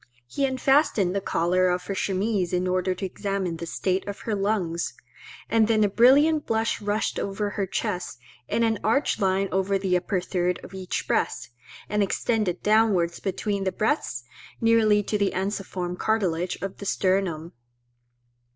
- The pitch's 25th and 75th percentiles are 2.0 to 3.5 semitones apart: Yes, average, 3.0 semitones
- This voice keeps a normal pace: Yes, average, 160 wpm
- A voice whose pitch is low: No, high, 195 Hz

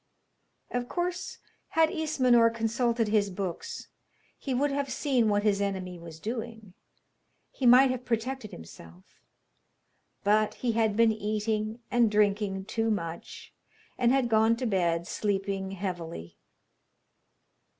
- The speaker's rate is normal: No, slow, 125 wpm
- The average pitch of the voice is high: Yes, high, 220 Hz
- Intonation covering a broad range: No, average, 3.7 semitones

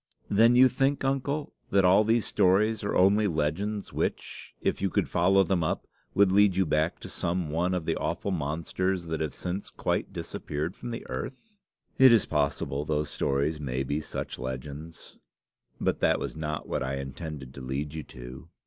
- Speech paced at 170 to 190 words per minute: Yes, average, 185 wpm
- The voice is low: Yes, very low, 85 Hz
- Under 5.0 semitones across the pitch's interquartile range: No, wide, 5.5 semitones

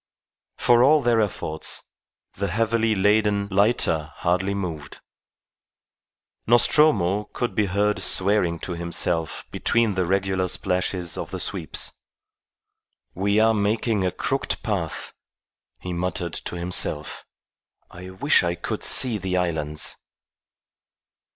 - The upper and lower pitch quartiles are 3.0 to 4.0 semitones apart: Yes, average, 3.5 semitones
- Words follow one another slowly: Yes, slow, 115 wpm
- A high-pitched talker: No, very low, 95 Hz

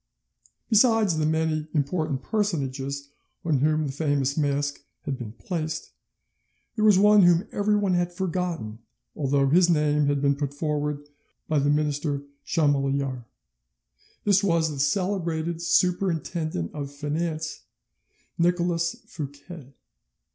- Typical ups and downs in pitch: Yes, average, 3.6 semitones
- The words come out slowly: Yes, slow, 120 wpm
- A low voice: No, medium, 155 Hz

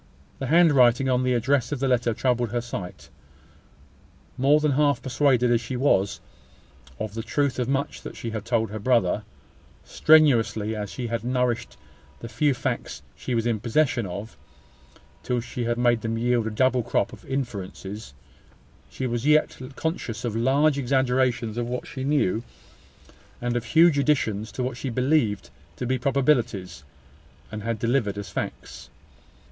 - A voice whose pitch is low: Yes, low, 120 Hz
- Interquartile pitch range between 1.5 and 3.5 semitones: Yes, average, 2.9 semitones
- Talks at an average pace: Yes, average, 165 wpm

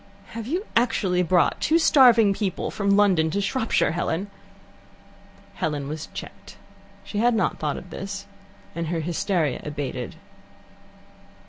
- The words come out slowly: Yes, slow, 130 wpm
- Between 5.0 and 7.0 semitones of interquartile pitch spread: Yes, wide, 5.4 semitones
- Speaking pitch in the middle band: No, high, 195 Hz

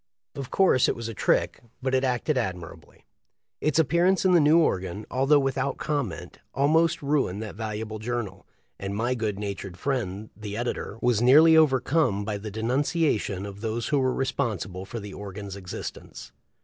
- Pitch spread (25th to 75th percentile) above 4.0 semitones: Yes, wide, 5.5 semitones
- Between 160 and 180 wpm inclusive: Yes, average, 165 wpm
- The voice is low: Yes, low, 120 Hz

